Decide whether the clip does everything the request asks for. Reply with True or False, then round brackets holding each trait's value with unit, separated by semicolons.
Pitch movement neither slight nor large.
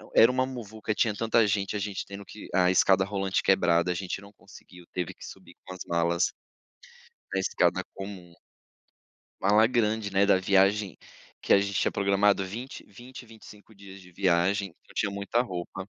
False (2.1 semitones)